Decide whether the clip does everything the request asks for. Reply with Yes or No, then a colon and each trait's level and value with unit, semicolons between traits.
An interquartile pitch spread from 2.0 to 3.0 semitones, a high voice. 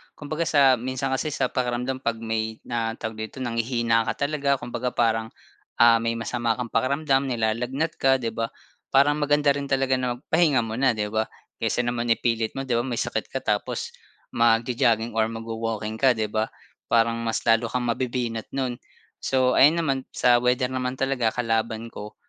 No: narrow, 2.6 semitones; low, 120 Hz